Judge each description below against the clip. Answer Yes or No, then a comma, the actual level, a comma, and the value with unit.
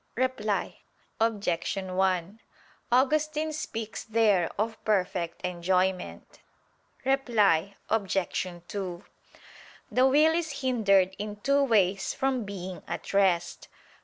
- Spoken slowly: Yes, slow, 100 wpm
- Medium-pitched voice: No, high, 205 Hz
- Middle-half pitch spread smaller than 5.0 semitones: No, wide, 5.4 semitones